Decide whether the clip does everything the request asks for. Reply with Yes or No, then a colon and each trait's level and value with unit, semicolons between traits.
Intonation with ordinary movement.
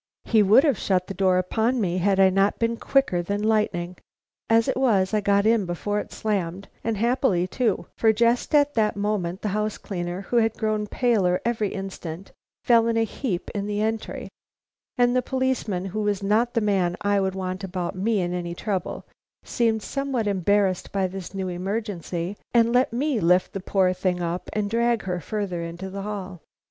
Yes: average, 3.5 semitones